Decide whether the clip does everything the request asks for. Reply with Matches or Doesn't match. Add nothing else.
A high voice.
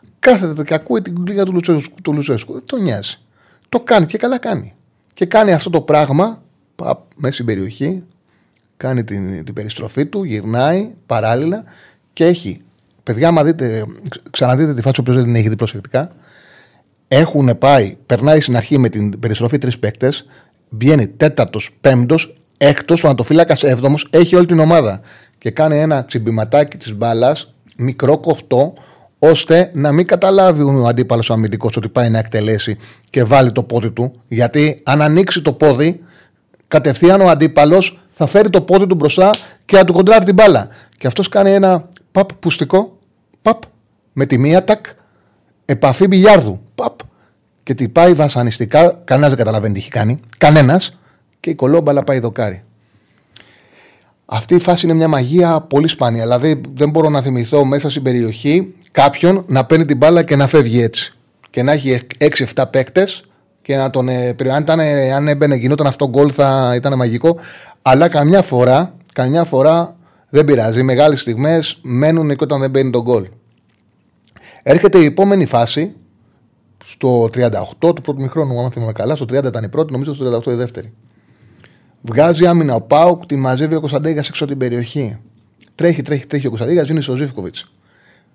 Doesn't match